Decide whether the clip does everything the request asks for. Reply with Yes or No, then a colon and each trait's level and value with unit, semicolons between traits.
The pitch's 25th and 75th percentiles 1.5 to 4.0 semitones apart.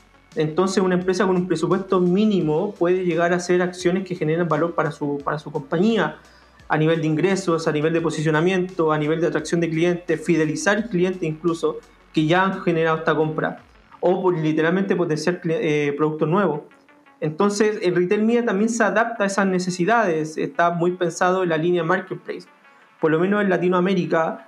Yes: average, 2.8 semitones